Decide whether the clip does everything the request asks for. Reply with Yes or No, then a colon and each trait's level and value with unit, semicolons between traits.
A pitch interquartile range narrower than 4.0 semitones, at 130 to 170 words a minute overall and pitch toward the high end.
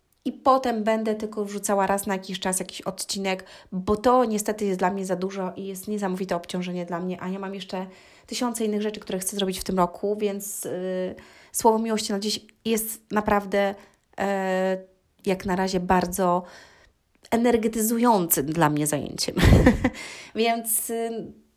Yes: average, 2.7 semitones; fast, 160 wpm; high, 195 Hz